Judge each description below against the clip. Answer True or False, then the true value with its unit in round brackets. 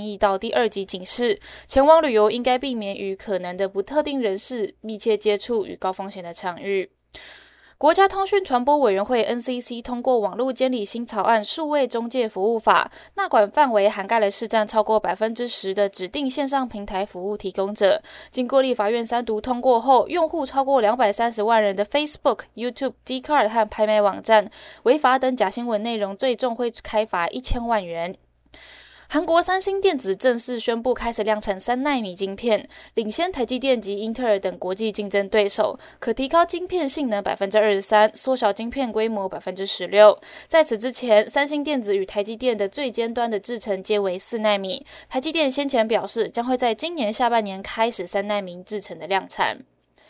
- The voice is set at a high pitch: True (230 Hz)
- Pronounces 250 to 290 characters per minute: False (315 characters per minute)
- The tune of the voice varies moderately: True (4.4 semitones)